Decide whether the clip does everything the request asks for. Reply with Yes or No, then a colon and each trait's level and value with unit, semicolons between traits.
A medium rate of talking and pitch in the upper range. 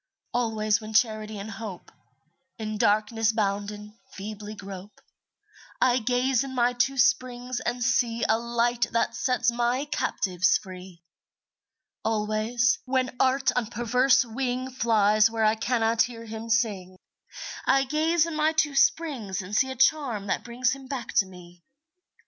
Yes: average, 145 wpm; high, 230 Hz